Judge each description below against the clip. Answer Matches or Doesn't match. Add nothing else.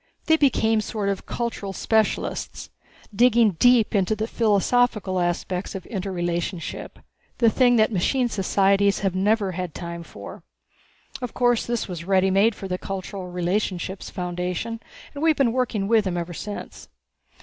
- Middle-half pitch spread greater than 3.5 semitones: Matches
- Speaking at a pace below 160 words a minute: Matches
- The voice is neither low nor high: Doesn't match